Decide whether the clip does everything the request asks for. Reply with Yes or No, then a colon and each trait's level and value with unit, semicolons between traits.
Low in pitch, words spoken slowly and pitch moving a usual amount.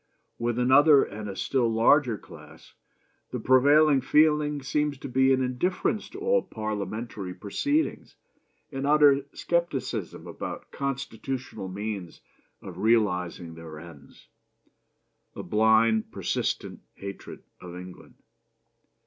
No: low, 120 Hz; slow, 110 wpm; wide, 5.8 semitones